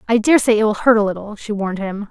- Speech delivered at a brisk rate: Yes, fast, 285 wpm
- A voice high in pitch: Yes, high, 215 Hz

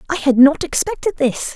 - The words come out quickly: No, average, 195 wpm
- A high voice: Yes, very high, 300 Hz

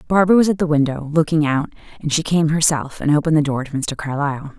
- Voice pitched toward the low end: No, medium, 150 Hz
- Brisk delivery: Yes, fast, 235 wpm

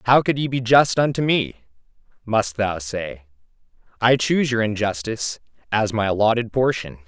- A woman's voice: No, male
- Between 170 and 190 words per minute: No, slow, 135 wpm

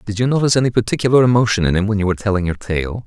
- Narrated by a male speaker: Yes, male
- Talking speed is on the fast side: Yes, fast, 275 wpm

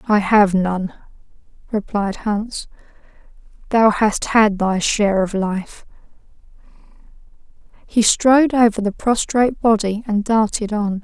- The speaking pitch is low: No, high, 210 Hz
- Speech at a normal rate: No, slow, 115 wpm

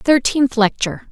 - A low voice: No, very high, 250 Hz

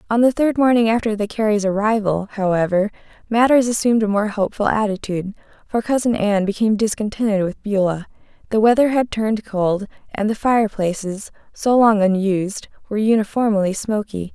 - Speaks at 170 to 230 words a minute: No, average, 150 wpm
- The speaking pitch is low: No, high, 210 Hz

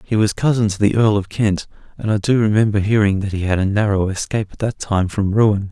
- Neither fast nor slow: No, fast, 250 wpm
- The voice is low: Yes, low, 105 Hz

